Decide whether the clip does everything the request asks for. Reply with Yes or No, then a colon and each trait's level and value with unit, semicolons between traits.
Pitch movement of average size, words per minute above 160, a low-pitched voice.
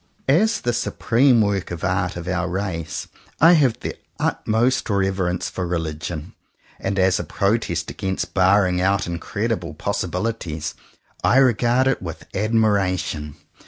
No: average, 4.3 semitones; average, 140 wpm; very low, 95 Hz